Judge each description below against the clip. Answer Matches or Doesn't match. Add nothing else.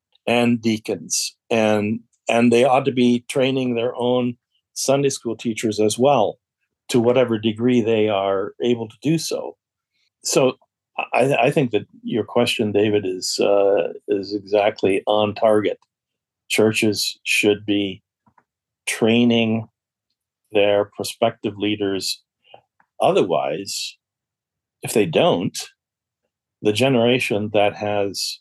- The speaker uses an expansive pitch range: Doesn't match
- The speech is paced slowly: Matches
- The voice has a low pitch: Matches